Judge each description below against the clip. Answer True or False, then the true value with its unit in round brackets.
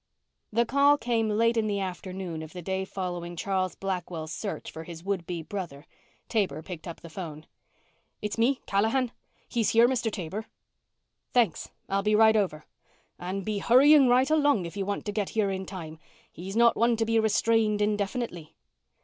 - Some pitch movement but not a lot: True (4.1 semitones)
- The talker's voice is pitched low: False (200 Hz)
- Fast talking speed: False (175 wpm)